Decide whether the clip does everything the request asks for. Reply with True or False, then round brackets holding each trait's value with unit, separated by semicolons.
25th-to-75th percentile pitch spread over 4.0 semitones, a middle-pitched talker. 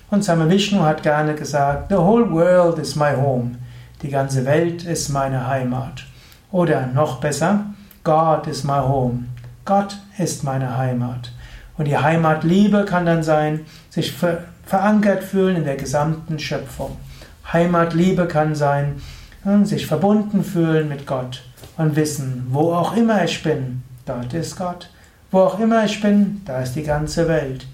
True (4.5 semitones; 155 Hz)